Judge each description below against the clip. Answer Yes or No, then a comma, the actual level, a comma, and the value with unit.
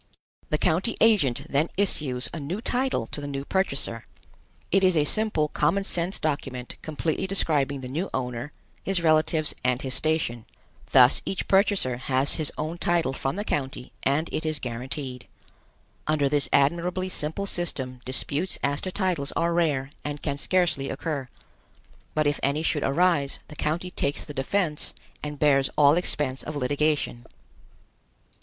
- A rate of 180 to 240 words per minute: No, average, 155 wpm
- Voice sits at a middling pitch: Yes, medium, 150 Hz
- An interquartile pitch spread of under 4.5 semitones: Yes, average, 4.0 semitones